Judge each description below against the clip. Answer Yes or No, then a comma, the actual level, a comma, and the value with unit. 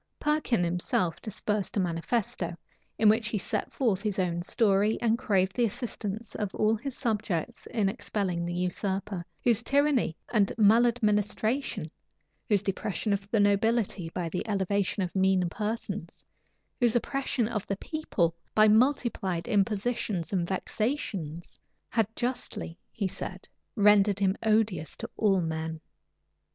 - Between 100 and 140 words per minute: Yes, slow, 135 wpm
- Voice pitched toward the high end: Yes, high, 205 Hz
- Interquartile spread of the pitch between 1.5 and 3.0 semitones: No, average, 3.4 semitones